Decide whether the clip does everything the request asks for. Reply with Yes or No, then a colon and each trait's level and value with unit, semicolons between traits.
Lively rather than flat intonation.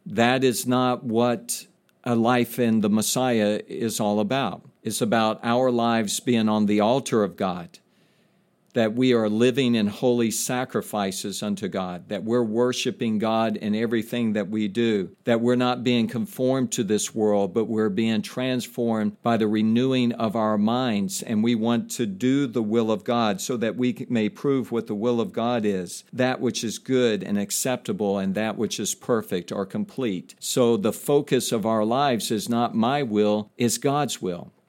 No: narrow, 2.6 semitones